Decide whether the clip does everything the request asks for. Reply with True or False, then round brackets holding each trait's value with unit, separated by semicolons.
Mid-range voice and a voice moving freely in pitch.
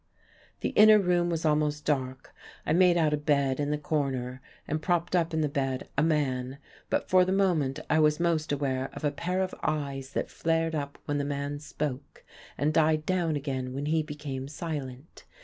False (150 Hz; 2.8 semitones)